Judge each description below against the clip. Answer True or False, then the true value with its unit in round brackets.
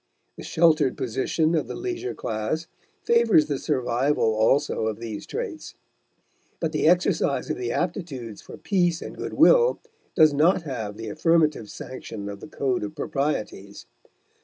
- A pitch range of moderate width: False (6.8 semitones)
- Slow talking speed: False (150 wpm)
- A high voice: False (150 Hz)